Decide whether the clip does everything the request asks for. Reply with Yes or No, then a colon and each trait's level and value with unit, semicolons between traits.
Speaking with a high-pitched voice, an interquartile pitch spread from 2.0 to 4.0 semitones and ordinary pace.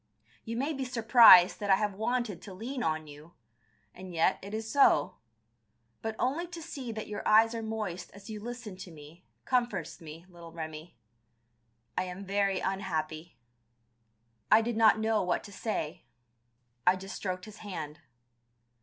No: high, 200 Hz; average, 4.4 semitones; average, 165 wpm